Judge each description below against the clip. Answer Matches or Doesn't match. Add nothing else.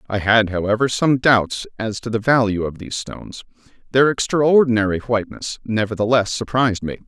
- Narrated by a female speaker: Doesn't match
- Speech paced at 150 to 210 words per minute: Matches